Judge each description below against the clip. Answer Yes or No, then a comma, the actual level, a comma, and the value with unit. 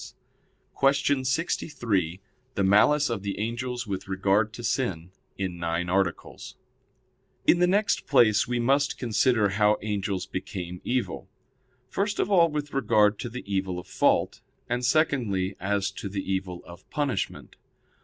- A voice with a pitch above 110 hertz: No, low, 105 Hz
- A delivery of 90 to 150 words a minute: Yes, average, 145 wpm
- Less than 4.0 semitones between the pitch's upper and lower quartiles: No, wide, 5.4 semitones